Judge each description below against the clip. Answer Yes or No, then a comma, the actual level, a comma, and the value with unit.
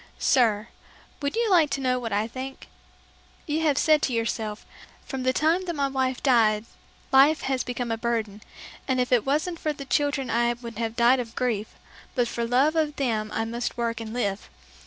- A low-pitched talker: No, very high, 250 Hz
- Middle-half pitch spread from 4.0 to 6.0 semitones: No, average, 3.4 semitones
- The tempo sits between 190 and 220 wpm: Yes, average, 200 wpm